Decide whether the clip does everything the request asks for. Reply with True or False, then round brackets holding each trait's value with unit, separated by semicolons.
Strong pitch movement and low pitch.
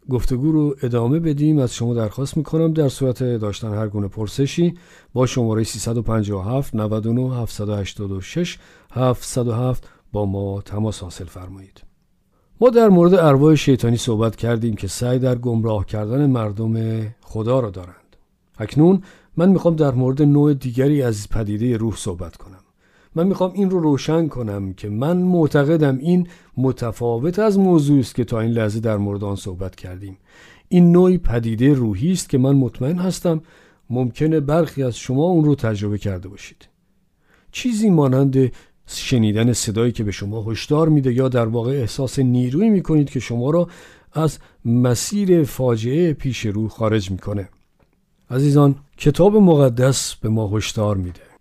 True (5.7 semitones; 125 Hz)